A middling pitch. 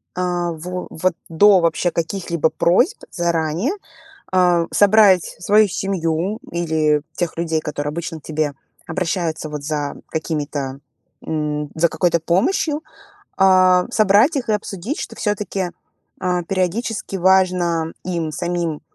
Yes: medium, 175 Hz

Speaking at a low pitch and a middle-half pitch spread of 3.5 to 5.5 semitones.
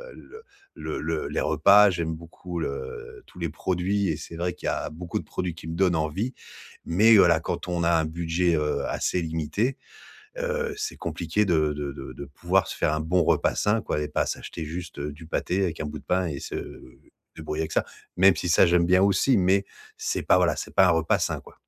No: very low, 85 Hz; average, 3.0 semitones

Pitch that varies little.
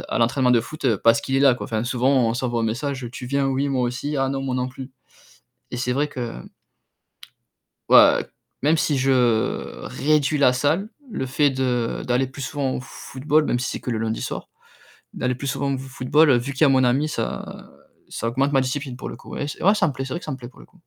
Yes: narrow, 2.2 semitones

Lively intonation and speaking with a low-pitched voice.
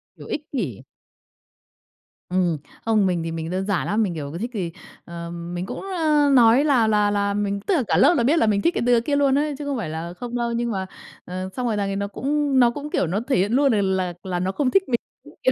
No: wide, 6.3 semitones; high, 210 Hz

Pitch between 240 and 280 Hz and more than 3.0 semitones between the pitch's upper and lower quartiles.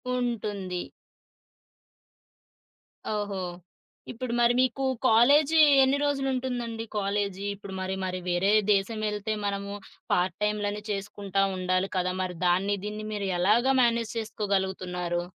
No: high, 205 Hz; average, 3.4 semitones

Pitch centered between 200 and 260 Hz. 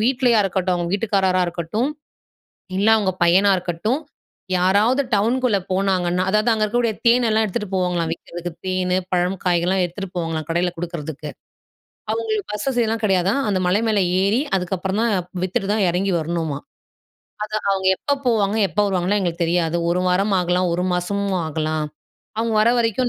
No: high, 190 Hz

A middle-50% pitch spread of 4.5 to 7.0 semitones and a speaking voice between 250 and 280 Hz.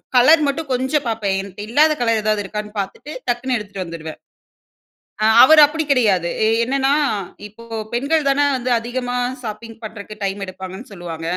No: average, 4.8 semitones; high, 225 Hz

